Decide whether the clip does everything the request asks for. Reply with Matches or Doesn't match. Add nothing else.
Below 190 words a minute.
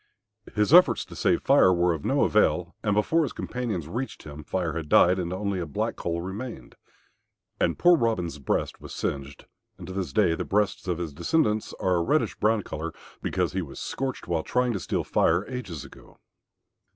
Doesn't match